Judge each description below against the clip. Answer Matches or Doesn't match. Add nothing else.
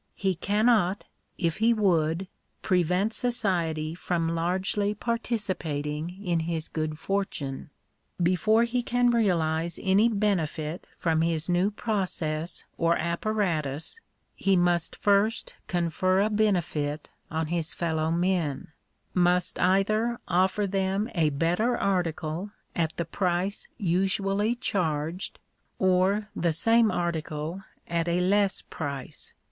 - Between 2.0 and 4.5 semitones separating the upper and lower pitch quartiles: Matches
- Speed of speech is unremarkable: Doesn't match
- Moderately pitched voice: Matches